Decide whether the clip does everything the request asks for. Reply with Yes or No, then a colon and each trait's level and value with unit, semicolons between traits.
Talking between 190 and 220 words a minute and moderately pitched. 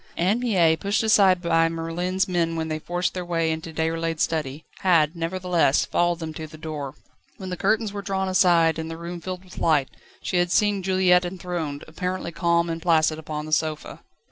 Yes: average, 195 wpm; medium, 170 Hz